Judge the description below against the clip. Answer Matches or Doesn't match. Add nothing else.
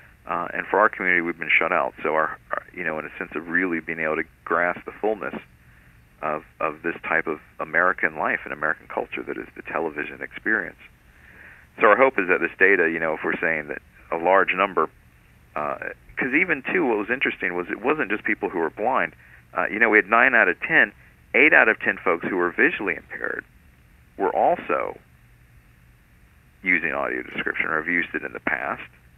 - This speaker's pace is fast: Matches